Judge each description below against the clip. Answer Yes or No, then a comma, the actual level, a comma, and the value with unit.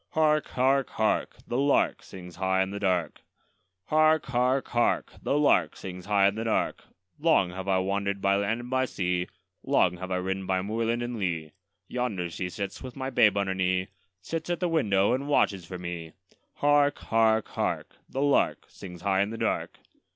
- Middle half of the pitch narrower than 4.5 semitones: No, wide, 5.6 semitones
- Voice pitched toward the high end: No, low, 100 Hz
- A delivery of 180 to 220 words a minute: Yes, average, 190 wpm